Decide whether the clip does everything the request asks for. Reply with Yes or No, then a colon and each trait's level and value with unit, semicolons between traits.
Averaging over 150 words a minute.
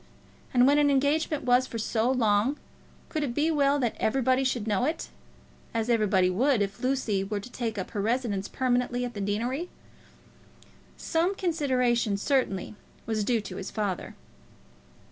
Yes: average, 160 wpm